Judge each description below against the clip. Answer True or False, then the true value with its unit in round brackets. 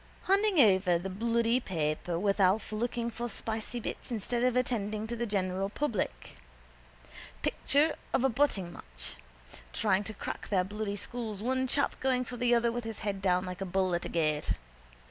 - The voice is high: True (215 Hz)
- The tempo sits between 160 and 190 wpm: True (180 wpm)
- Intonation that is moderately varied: True (4.1 semitones)